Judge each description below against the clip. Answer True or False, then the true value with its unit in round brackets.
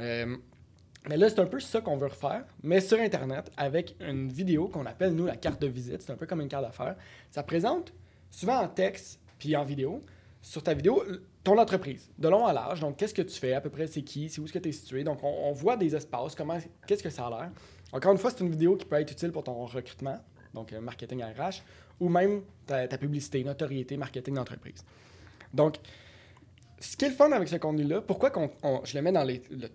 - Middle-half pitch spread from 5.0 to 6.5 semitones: True (5.3 semitones)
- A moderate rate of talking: False (240 wpm)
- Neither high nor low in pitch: True (145 Hz)